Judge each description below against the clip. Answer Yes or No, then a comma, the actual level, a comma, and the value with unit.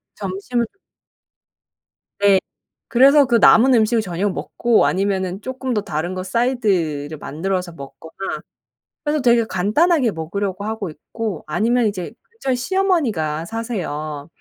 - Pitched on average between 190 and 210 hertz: Yes, high, 205 Hz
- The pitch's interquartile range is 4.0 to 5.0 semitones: No, wide, 5.4 semitones